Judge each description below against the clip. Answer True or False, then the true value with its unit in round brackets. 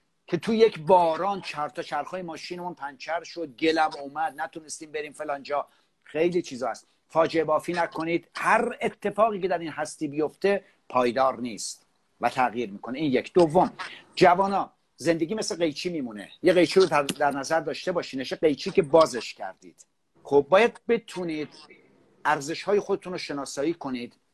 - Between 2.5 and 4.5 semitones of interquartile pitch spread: True (3.8 semitones)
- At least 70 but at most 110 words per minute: False (150 wpm)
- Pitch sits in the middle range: True (165 Hz)